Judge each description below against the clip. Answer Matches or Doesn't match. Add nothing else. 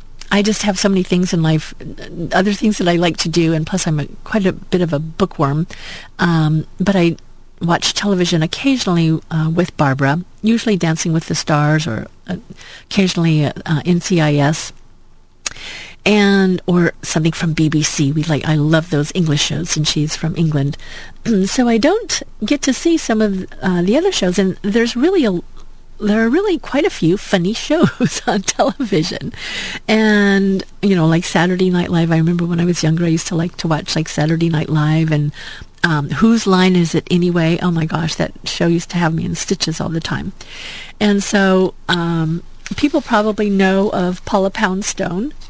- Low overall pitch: Doesn't match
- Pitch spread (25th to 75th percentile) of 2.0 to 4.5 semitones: Matches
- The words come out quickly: Doesn't match